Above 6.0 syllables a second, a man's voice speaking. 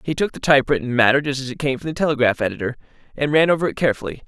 Yes: 8.0 syllables/s; male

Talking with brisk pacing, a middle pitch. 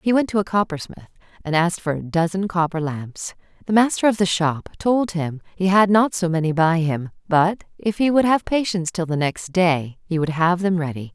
Yes: fast, 220 wpm; medium, 180 Hz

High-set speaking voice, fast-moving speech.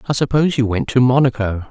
No: low, 125 Hz; fast, 210 wpm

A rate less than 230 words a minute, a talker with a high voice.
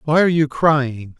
No: average, 200 wpm; medium, 145 Hz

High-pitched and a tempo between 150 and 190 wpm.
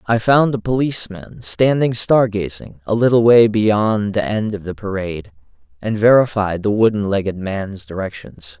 No: low, 105 Hz; average, 160 wpm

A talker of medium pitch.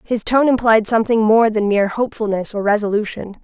No: high, 220 Hz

